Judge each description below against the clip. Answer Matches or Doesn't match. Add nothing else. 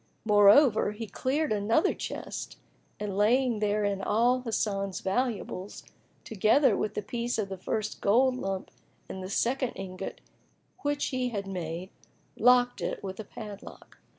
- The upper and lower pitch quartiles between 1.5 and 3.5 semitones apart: Doesn't match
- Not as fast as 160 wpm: Matches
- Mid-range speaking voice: Doesn't match